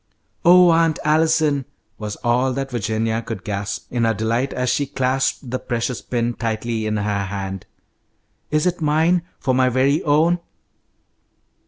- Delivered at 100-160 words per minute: Yes, average, 150 wpm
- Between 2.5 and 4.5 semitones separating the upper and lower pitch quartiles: No, average, 5.1 semitones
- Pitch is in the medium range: No, low, 125 Hz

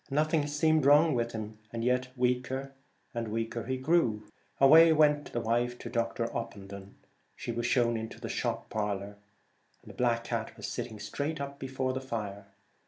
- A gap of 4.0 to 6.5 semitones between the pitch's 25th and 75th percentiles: No, average, 3.6 semitones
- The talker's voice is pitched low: Yes, low, 120 Hz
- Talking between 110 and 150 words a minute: No, average, 165 wpm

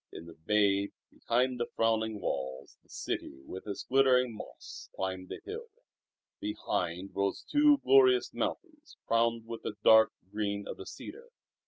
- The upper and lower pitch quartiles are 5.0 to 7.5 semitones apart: Yes, wide, 5.6 semitones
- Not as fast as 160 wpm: Yes, average, 150 wpm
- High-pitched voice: No, low, 110 Hz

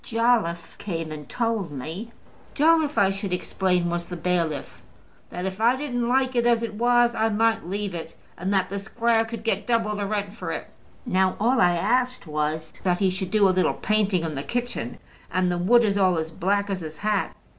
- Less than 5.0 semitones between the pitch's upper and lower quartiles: Yes, average, 4.5 semitones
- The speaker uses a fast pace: Yes, fast, 210 wpm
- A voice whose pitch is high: Yes, high, 200 Hz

